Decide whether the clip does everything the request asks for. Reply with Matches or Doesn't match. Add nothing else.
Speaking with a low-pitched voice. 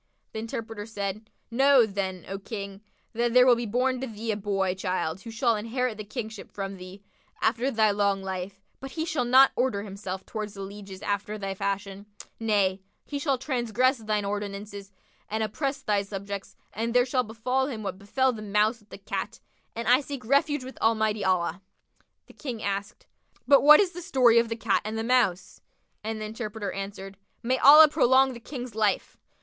Doesn't match